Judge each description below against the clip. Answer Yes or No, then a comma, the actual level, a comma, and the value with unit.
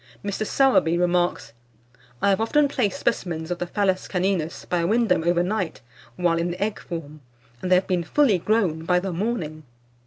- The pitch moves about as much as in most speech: Yes, average, 3.2 semitones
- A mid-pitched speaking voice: Yes, medium, 180 Hz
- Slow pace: No, average, 185 wpm